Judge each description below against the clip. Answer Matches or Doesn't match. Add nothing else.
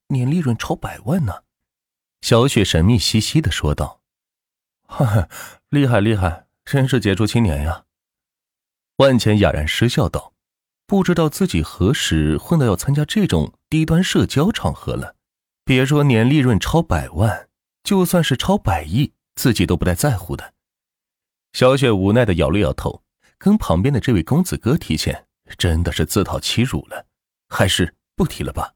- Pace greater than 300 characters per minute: Doesn't match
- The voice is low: Matches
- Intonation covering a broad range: Matches